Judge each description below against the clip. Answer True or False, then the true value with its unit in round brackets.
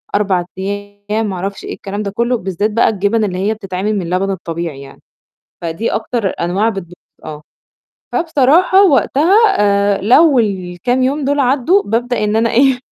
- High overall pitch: True (210 Hz)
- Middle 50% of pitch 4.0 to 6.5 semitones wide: True (4.5 semitones)